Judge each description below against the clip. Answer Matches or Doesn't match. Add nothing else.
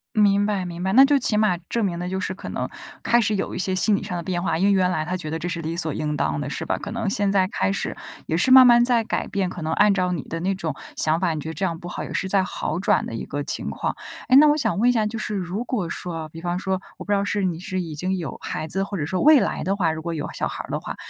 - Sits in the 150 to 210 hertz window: Matches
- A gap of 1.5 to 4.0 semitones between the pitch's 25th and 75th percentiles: Matches